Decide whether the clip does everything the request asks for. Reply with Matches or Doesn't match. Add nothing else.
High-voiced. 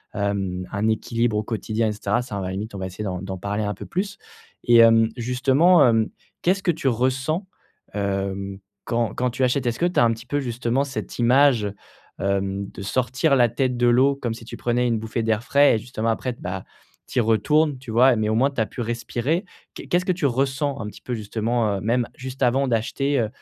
Doesn't match